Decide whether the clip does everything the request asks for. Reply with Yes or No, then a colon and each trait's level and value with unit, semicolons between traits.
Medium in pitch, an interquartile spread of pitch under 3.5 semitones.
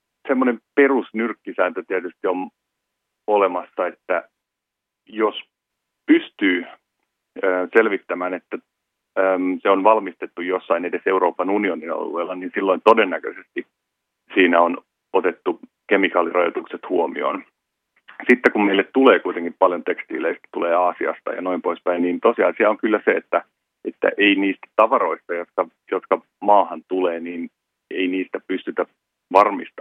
No: very low, 95 Hz; average, 2.8 semitones